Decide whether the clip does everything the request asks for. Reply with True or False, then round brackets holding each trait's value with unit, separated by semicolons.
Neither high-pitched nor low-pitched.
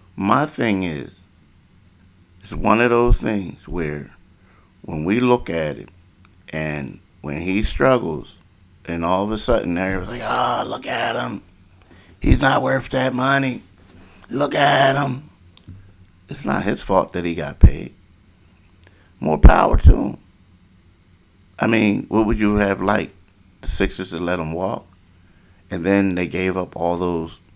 False (95 Hz)